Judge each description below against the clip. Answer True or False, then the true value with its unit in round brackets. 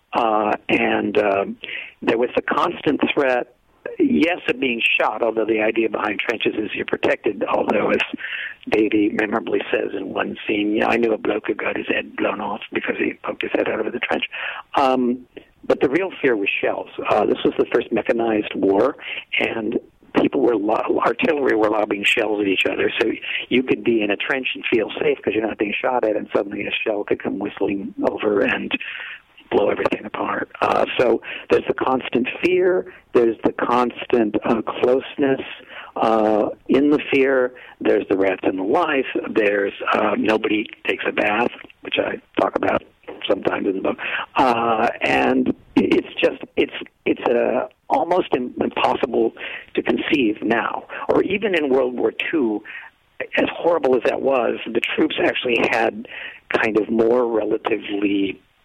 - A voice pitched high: False (130 Hz)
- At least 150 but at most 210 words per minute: True (170 wpm)